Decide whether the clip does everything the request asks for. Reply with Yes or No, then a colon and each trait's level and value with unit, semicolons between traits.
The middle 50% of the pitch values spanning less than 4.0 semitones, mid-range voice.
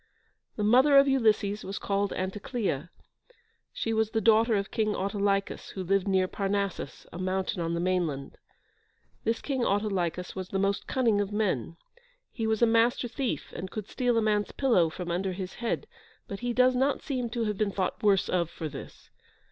No: average, 3.5 semitones; high, 205 Hz